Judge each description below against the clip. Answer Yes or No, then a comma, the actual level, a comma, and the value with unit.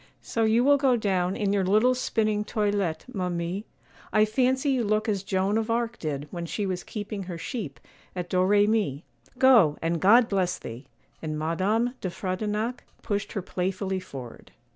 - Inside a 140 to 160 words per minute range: No, average, 170 wpm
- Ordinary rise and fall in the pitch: Yes, average, 3.6 semitones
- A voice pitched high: Yes, high, 200 Hz